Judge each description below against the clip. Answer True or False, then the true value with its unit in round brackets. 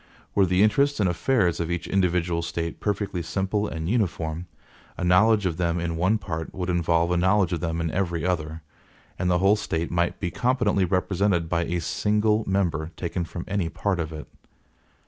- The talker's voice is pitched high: False (90 Hz)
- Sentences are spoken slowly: False (185 wpm)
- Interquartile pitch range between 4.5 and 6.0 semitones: False (2.9 semitones)